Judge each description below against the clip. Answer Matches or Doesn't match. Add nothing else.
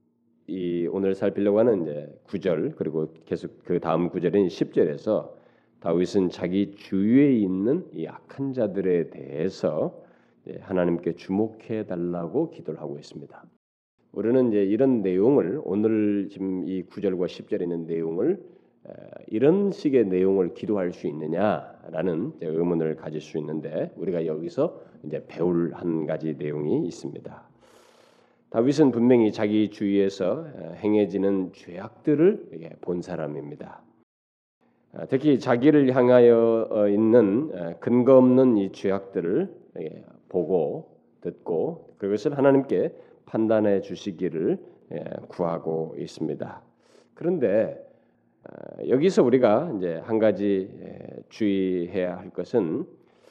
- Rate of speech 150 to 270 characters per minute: Matches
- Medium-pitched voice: Doesn't match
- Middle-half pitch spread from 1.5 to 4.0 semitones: Doesn't match